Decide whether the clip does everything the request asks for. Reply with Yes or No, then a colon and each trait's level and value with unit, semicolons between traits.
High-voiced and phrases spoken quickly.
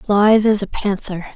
No: high, 205 Hz; average, 175 wpm